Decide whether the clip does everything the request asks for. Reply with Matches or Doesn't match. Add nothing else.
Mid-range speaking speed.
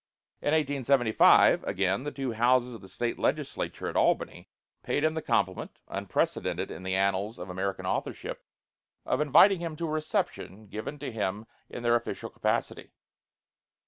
Matches